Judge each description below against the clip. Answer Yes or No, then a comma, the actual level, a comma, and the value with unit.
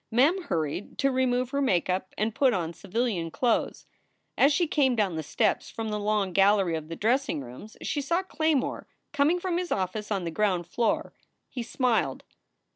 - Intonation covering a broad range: Yes, wide, 6.7 semitones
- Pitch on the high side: Yes, high, 225 Hz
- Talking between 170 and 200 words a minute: Yes, average, 180 wpm